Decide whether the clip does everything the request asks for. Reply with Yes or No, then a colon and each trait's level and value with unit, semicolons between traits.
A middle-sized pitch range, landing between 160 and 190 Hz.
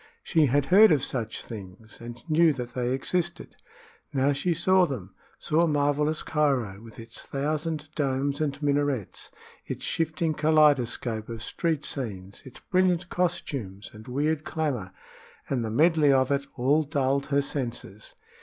No: average, 4.3 semitones; medium, 140 Hz